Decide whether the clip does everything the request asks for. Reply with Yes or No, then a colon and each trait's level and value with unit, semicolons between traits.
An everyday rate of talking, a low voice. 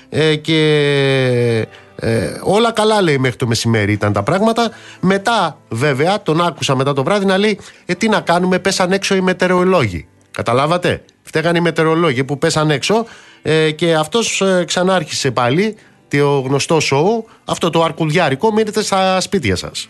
No: average, 155 wpm; medium, 165 Hz